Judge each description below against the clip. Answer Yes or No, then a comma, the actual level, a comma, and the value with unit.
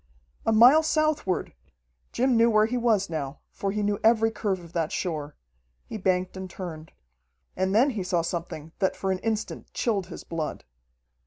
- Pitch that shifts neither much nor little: Yes, average, 4.4 semitones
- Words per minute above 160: Yes, average, 175 wpm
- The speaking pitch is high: Yes, high, 195 Hz